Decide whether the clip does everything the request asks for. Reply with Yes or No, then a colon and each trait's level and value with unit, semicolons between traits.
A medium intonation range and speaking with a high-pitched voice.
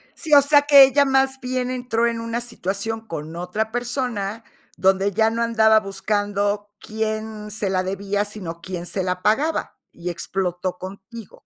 Yes: average, 3.5 semitones; high, 215 Hz